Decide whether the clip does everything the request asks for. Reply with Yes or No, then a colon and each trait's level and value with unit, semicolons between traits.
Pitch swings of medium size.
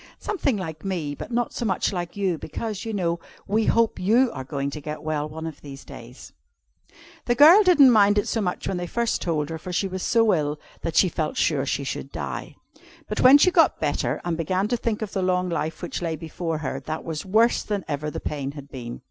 No: wide, 6.0 semitones